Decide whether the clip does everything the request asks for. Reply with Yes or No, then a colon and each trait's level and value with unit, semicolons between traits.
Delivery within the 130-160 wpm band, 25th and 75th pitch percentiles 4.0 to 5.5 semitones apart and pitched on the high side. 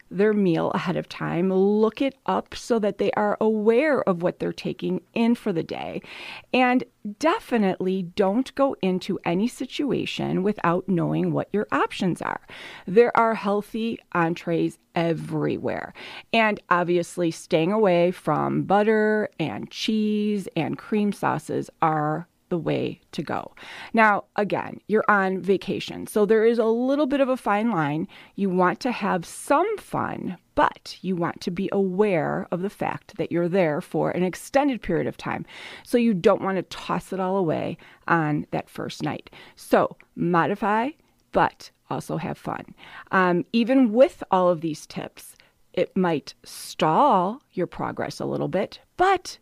Yes: average, 155 wpm; average, 4.3 semitones; high, 195 Hz